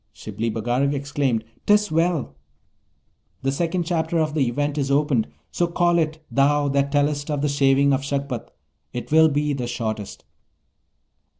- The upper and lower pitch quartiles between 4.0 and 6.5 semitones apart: No, narrow, 2.5 semitones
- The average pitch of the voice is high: No, medium, 145 Hz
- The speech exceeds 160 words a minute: No, average, 155 wpm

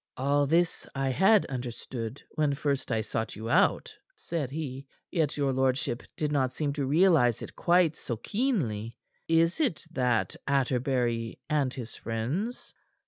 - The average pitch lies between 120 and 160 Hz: Yes, medium, 140 Hz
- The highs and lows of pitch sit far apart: No, average, 4.7 semitones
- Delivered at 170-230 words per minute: No, average, 145 wpm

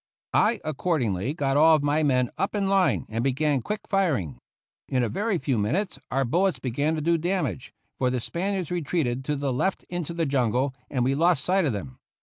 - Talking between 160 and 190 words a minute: No, average, 200 wpm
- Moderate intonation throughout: No, wide, 5.7 semitones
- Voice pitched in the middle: Yes, medium, 145 Hz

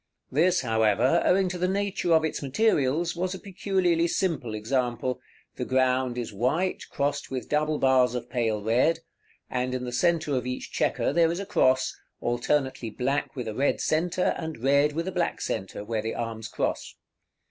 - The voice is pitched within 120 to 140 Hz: Yes, low, 135 Hz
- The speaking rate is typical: Yes, average, 180 wpm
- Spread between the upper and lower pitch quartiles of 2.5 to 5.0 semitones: No, wide, 5.5 semitones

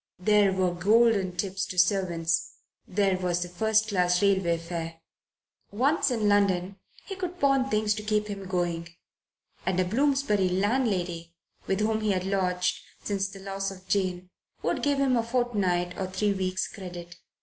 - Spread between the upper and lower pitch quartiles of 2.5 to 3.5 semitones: Yes, average, 2.9 semitones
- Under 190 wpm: Yes, average, 160 wpm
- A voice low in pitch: No, high, 195 Hz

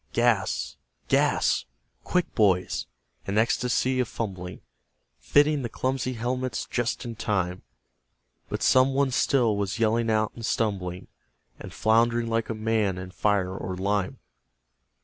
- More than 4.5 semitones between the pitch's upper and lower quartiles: No, average, 3.7 semitones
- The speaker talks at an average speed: No, slow, 130 wpm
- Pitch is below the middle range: Yes, low, 115 Hz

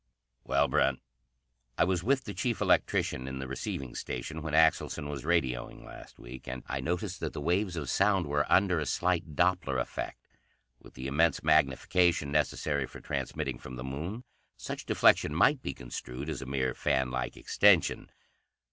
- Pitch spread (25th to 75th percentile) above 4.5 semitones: Yes, average, 4.9 semitones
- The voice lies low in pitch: Yes, very low, 75 Hz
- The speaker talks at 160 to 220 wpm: Yes, average, 170 wpm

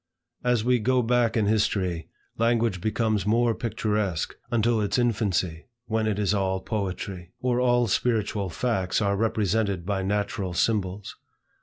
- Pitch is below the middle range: Yes, low, 105 Hz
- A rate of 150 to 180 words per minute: No, average, 140 wpm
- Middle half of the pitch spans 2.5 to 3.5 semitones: Yes, average, 3.2 semitones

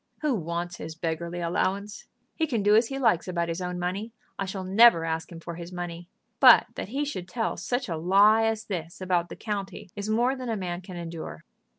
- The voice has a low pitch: No, medium, 185 Hz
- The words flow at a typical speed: No, fast, 220 wpm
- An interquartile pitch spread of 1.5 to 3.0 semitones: No, average, 4.3 semitones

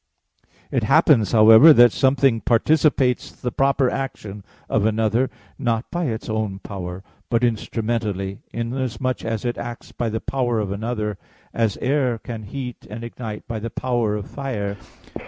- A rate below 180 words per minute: Yes, average, 150 wpm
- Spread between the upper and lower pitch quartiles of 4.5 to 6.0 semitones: No, average, 2.8 semitones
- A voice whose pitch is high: No, low, 115 Hz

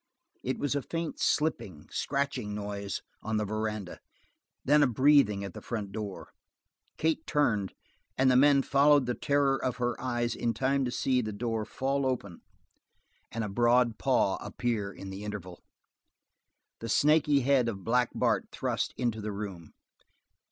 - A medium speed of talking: Yes, average, 160 wpm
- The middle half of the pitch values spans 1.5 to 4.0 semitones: No, average, 4.7 semitones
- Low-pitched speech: Yes, low, 120 Hz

